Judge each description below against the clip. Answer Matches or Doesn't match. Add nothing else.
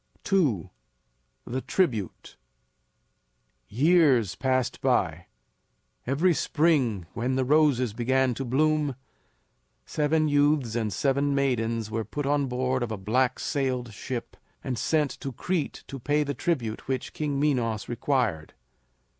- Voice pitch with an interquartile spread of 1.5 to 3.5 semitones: Doesn't match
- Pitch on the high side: Doesn't match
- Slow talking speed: Matches